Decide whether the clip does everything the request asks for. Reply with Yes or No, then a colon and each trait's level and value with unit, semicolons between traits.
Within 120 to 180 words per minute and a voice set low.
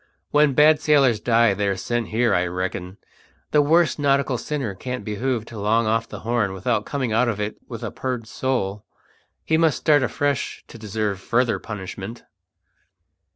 Yes: average, 170 wpm; low, 115 Hz